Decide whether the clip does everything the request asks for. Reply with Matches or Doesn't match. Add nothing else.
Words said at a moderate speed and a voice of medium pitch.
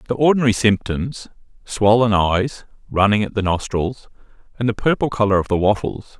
Doesn't match